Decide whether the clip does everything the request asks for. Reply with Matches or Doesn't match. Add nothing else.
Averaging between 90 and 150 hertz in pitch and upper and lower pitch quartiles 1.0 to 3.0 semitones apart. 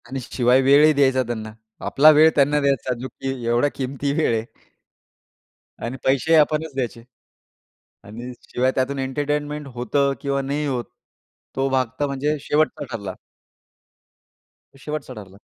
Matches